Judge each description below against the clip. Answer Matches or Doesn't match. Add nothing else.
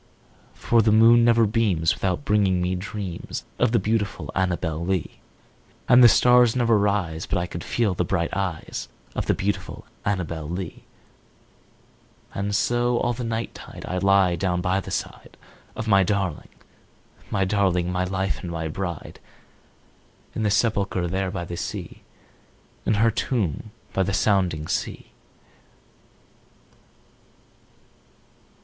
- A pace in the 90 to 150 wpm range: Matches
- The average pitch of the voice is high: Doesn't match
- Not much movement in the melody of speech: Doesn't match